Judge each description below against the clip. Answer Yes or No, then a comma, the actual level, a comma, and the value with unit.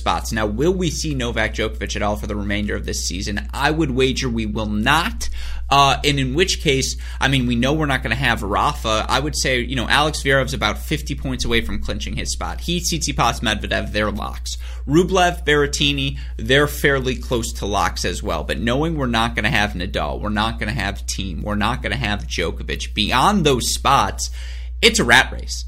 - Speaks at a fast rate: Yes, fast, 215 wpm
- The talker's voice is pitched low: Yes, low, 110 Hz